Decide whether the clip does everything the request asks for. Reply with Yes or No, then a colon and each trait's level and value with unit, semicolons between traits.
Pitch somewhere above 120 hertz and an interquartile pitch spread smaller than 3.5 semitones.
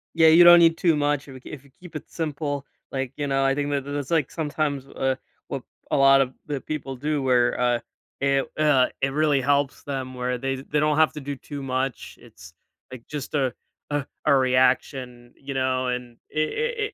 Yes: medium, 140 Hz; narrow, 2.4 semitones